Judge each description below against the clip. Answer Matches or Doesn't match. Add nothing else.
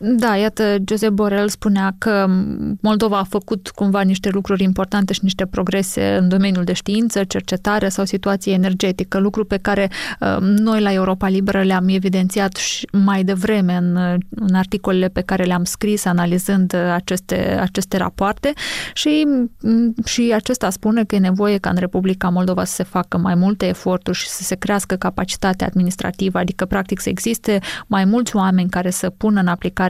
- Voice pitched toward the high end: Matches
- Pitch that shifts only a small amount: Matches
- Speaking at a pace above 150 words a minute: Matches